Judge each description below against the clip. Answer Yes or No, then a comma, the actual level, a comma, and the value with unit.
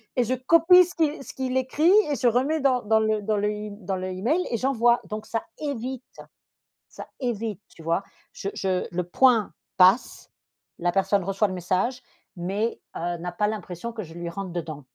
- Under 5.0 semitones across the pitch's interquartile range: No, wide, 5.5 semitones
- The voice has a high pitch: Yes, high, 215 Hz